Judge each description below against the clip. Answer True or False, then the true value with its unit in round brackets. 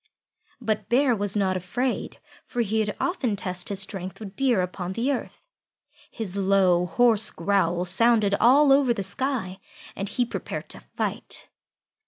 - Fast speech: False (155 wpm)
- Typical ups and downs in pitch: True (4.4 semitones)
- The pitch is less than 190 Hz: False (205 Hz)